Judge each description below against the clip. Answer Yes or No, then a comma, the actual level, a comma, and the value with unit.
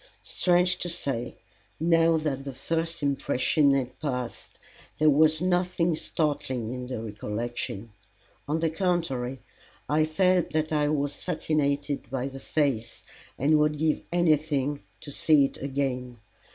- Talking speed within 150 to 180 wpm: No, slow, 135 wpm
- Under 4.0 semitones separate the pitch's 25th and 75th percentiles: Yes, average, 3.4 semitones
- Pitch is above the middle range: No, medium, 145 Hz